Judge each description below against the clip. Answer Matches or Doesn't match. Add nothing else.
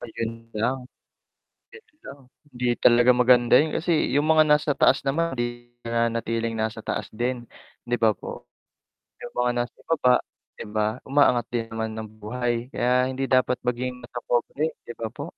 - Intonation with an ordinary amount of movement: Doesn't match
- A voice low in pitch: Matches